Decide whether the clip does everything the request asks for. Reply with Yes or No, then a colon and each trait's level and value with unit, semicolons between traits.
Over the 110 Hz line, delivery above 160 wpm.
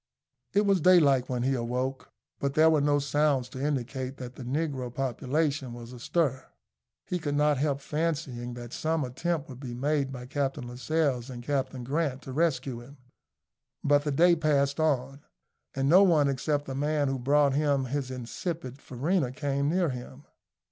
Yes: medium, 140 Hz; average, 170 wpm